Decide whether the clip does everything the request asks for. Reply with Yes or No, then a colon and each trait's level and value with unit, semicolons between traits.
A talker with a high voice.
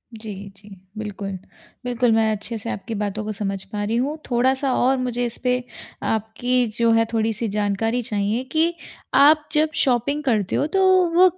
Yes: high, 230 Hz